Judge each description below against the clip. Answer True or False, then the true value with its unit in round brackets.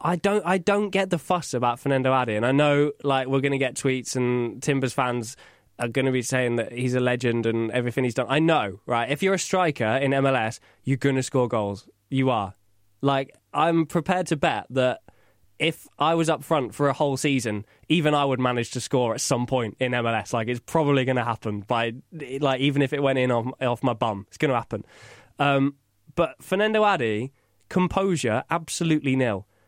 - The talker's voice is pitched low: True (130 Hz)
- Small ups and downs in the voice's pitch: False (3.8 semitones)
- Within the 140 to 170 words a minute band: False (200 wpm)